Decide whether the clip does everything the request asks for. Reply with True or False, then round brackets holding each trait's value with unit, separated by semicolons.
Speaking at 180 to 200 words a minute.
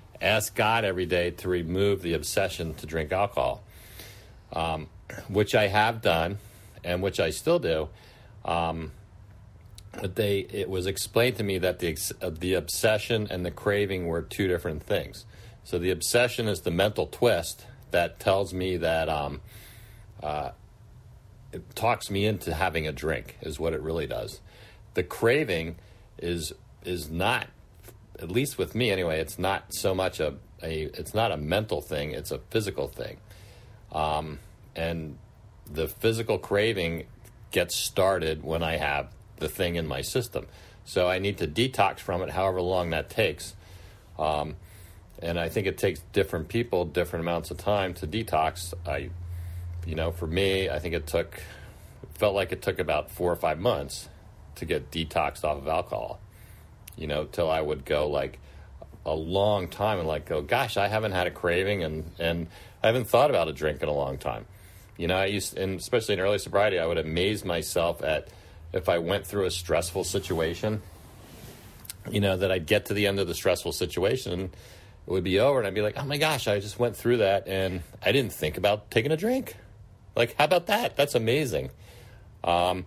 True (185 wpm)